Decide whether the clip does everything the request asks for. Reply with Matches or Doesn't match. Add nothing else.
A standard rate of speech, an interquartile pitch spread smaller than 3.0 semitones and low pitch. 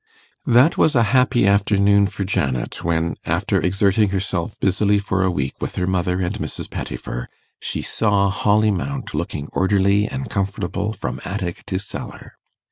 Matches